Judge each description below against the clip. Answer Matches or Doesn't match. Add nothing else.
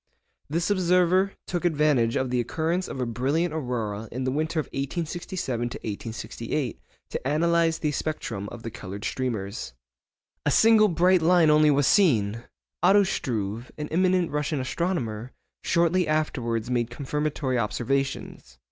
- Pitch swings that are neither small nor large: Doesn't match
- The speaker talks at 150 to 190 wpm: Doesn't match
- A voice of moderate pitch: Matches